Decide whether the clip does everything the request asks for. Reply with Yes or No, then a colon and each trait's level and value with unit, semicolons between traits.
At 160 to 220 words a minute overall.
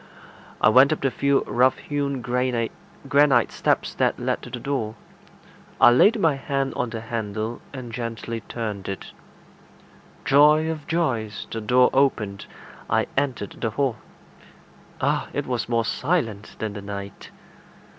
No: average, 145 wpm